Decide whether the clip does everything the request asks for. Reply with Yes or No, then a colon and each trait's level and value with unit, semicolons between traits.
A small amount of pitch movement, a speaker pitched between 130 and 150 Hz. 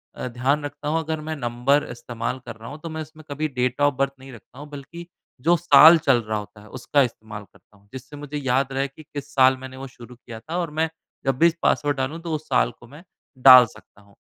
No: average, 3.7 semitones; low, 135 Hz